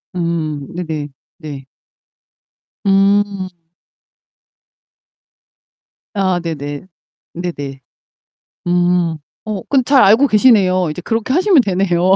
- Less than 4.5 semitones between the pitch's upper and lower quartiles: Yes, average, 3.9 semitones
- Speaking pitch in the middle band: Yes, medium, 180 Hz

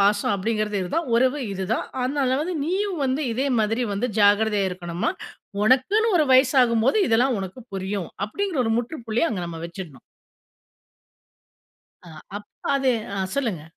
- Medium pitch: No, high, 230 Hz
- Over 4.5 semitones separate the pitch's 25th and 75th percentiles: Yes, average, 5.2 semitones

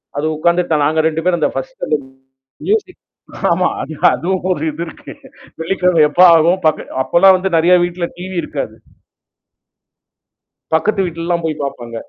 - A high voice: No, medium, 170 Hz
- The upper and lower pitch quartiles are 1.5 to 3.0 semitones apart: Yes, average, 2.7 semitones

